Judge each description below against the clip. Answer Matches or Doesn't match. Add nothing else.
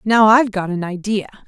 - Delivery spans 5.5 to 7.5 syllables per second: Matches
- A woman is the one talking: Matches